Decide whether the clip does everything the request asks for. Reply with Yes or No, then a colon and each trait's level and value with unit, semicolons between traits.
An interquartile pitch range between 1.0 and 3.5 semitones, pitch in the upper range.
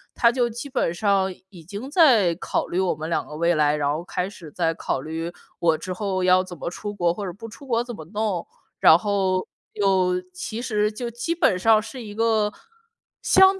No: average, 4.5 semitones; high, 195 Hz